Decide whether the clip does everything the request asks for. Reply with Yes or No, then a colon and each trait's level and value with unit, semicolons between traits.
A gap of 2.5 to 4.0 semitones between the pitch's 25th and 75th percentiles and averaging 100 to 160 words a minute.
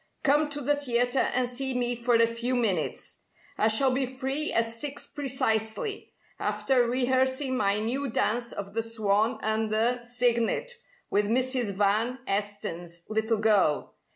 Yes: average, 3.1 semitones; average, 150 wpm